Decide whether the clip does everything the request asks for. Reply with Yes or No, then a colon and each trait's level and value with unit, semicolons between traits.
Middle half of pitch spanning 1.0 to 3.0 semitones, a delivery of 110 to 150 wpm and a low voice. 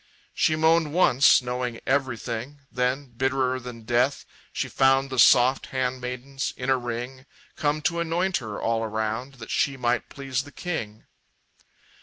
Yes: narrow, 2.4 semitones; average, 145 wpm; low, 130 Hz